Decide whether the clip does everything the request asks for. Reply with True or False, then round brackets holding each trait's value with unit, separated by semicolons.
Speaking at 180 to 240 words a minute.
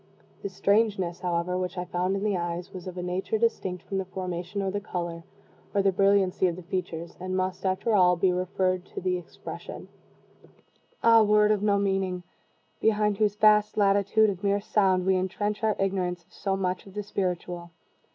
True (190 wpm)